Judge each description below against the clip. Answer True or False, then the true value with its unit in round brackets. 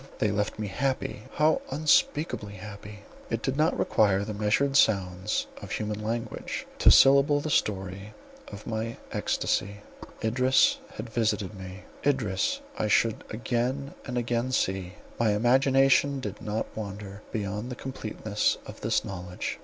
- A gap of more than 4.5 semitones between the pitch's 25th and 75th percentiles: False (4.1 semitones)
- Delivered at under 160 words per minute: True (135 wpm)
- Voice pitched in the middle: False (110 Hz)